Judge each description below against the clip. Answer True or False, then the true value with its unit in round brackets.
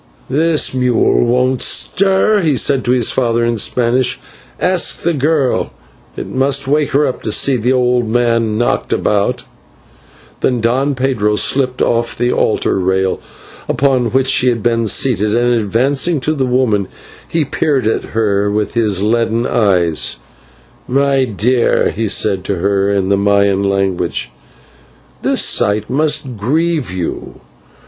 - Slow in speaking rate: False (145 wpm)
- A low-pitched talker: True (120 Hz)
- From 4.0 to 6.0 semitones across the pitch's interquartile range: True (4.3 semitones)